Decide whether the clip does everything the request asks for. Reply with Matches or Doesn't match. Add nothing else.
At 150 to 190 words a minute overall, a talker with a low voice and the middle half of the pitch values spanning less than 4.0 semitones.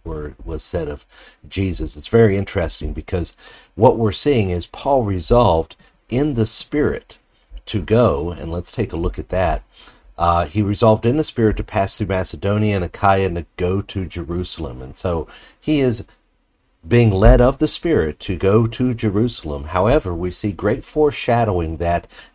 Doesn't match